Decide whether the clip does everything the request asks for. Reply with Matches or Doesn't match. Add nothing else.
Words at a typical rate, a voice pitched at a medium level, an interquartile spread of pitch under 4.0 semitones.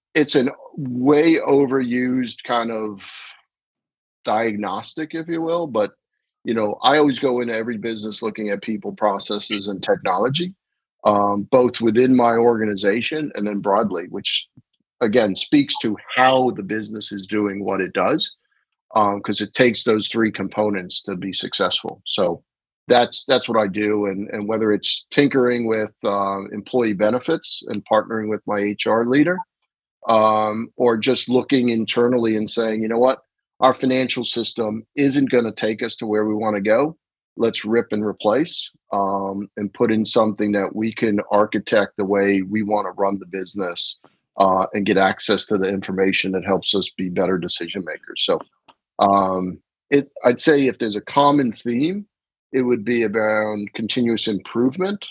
Doesn't match